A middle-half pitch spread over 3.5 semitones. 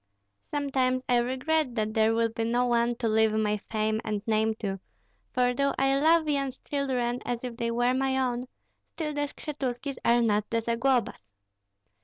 No: average, 3.0 semitones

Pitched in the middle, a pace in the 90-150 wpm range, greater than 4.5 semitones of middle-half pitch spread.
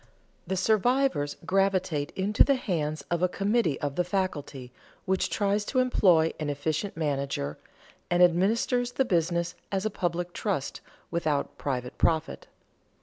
Yes: medium, 175 Hz; average, 140 wpm; average, 4.9 semitones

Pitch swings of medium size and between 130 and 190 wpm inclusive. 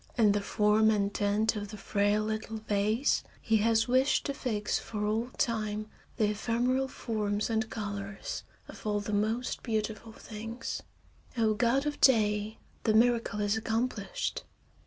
No: narrow, 1.8 semitones; average, 150 wpm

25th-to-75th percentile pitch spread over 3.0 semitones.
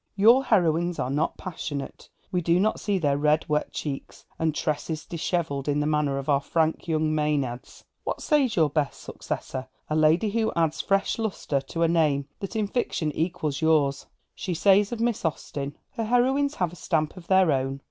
Yes: average, 4.7 semitones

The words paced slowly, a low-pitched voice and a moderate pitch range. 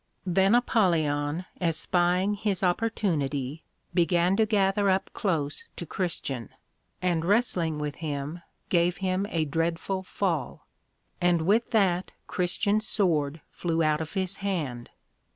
No: slow, 120 wpm; medium, 175 Hz; average, 3.6 semitones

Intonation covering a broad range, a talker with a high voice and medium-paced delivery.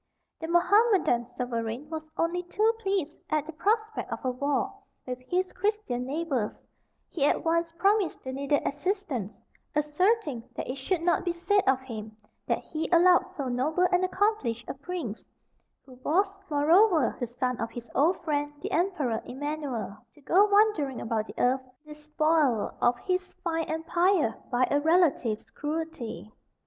Yes: wide, 6.1 semitones; very high, 305 Hz; average, 155 wpm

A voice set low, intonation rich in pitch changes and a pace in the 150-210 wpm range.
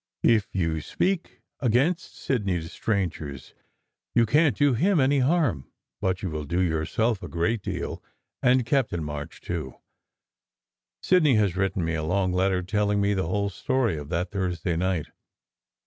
Yes: very low, 95 Hz; wide, 6.3 semitones; average, 160 wpm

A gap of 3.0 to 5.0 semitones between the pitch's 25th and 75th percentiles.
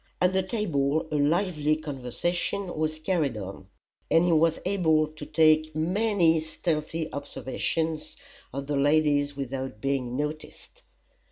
No: narrow, 2.6 semitones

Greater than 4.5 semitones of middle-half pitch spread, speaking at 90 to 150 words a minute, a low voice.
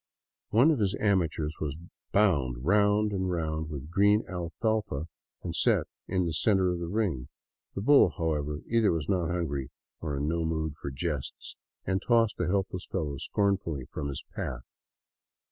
No: average, 5.1 semitones; average, 160 wpm; very low, 85 Hz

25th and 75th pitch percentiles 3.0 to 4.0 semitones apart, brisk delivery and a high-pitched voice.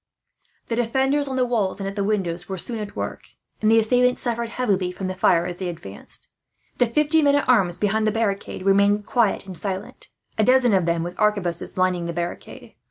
No: average, 4.4 semitones; fast, 210 wpm; high, 205 Hz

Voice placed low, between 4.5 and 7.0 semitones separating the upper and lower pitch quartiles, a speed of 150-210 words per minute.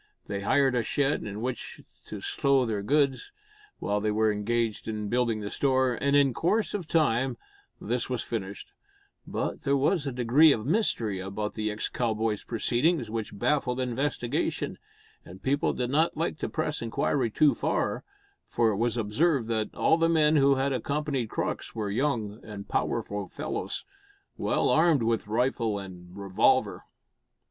Yes: low, 120 Hz; average, 4.9 semitones; average, 160 wpm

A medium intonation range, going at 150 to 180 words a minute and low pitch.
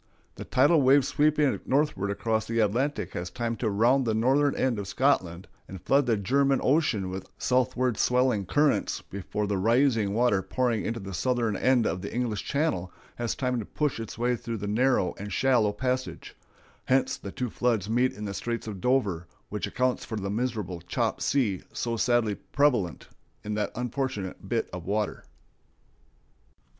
Yes: average, 4.2 semitones; average, 170 wpm; low, 115 Hz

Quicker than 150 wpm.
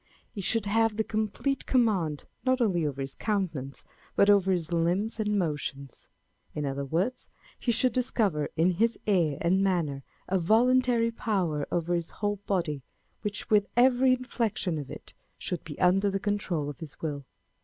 Yes: average, 165 wpm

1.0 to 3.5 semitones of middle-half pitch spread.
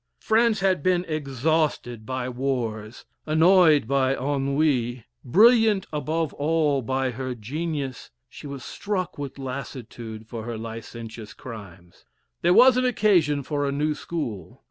No: average, 5.1 semitones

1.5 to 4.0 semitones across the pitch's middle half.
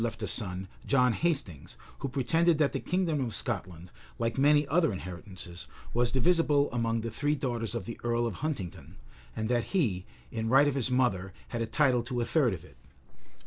No: average, 4.8 semitones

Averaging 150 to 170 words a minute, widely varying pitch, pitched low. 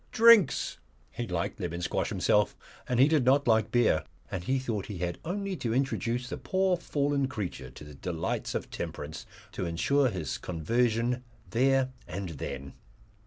Yes: average, 165 wpm; wide, 7.4 semitones; low, 120 Hz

